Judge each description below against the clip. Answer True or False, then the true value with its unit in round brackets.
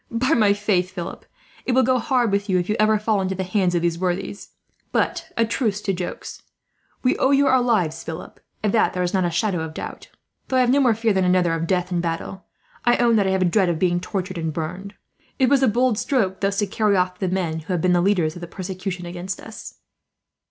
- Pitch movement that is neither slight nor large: True (3.9 semitones)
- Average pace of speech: False (250 wpm)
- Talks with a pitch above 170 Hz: True (190 Hz)